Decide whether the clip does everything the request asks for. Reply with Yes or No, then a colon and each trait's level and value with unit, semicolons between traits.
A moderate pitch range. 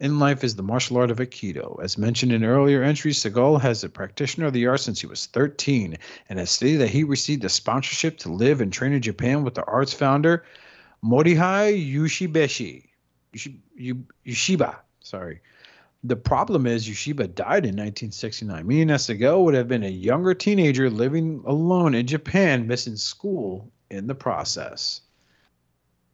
Yes: average, 5.0 semitones